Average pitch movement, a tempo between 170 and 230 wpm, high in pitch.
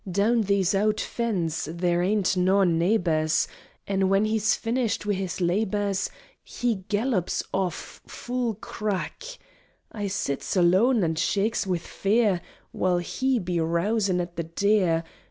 No: average, 3.4 semitones; slow, 135 wpm; high, 195 Hz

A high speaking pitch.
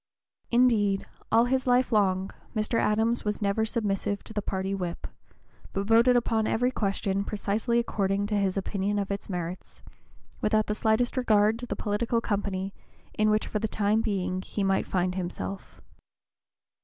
Yes: high, 210 Hz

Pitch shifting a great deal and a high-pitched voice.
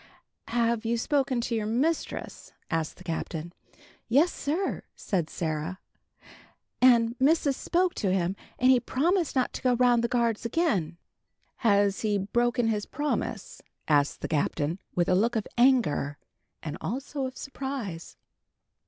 Yes: wide, 5.9 semitones; high, 235 Hz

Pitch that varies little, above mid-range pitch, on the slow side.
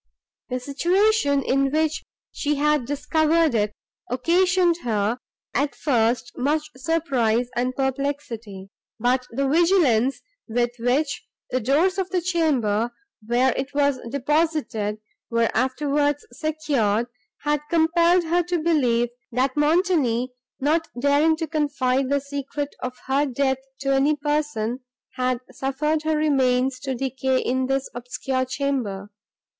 No: average, 3.6 semitones; very high, 275 Hz; slow, 125 wpm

